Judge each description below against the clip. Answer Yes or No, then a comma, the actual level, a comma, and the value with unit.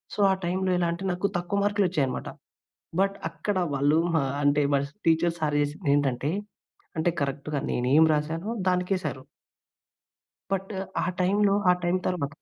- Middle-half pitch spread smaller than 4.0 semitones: No, average, 4.3 semitones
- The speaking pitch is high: No, medium, 170 Hz